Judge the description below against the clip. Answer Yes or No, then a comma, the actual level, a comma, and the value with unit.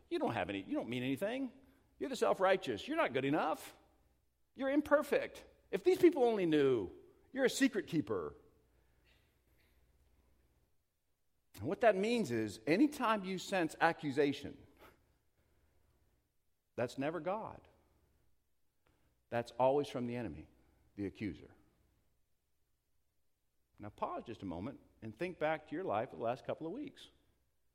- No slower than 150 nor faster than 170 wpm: No, slow, 135 wpm